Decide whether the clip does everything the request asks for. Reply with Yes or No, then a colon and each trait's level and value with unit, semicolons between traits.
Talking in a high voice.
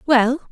Yes: very high, 260 Hz